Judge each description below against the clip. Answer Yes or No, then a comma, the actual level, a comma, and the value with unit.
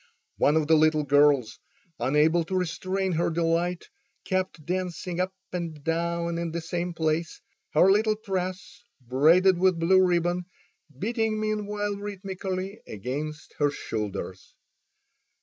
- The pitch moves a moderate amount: Yes, average, 3.2 semitones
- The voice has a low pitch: No, medium, 170 Hz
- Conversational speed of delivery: No, slow, 125 wpm